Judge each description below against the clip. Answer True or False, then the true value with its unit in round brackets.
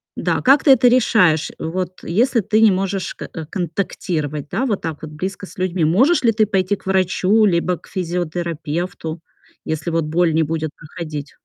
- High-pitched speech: False (180 Hz)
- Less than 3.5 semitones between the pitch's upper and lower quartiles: False (3.9 semitones)